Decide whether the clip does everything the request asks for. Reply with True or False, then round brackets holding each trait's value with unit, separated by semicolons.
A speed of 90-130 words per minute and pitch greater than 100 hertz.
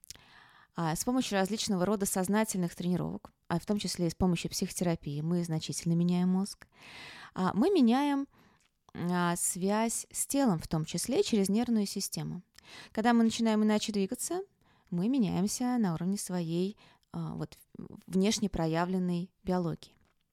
True (125 wpm; 190 Hz)